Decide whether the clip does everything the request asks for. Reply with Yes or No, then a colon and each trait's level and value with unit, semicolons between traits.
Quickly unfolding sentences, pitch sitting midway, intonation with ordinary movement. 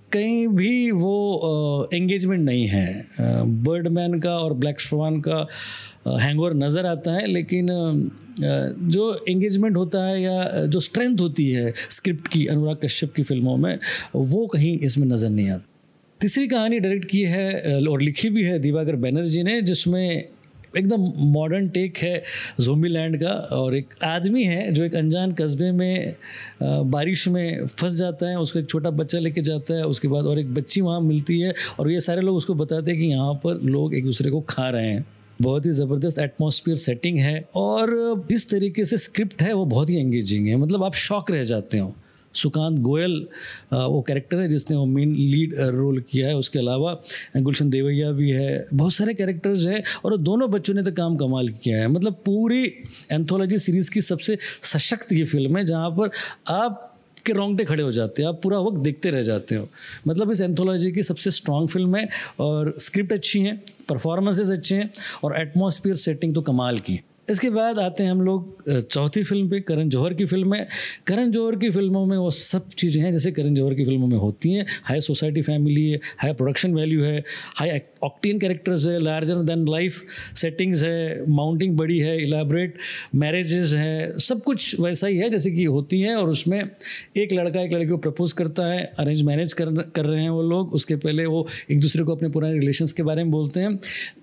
Yes: fast, 195 wpm; medium, 165 Hz; average, 4.3 semitones